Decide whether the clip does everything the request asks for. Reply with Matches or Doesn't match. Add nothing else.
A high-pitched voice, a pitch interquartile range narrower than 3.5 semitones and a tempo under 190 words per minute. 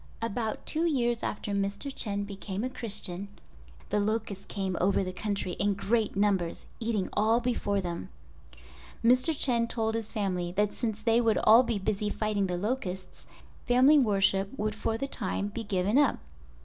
Matches